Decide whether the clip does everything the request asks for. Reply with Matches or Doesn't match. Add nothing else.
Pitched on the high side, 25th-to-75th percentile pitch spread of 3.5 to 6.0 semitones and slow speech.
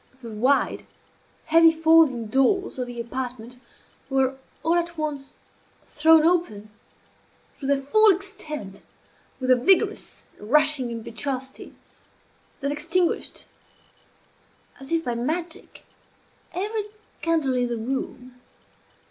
Matches